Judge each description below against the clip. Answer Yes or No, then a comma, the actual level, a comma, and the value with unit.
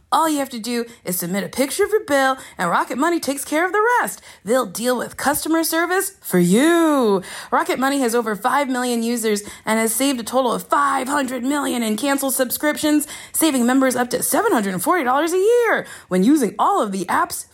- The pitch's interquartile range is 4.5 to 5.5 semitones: Yes, average, 5.1 semitones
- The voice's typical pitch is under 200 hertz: No, very high, 270 Hz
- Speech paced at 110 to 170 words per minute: No, average, 200 wpm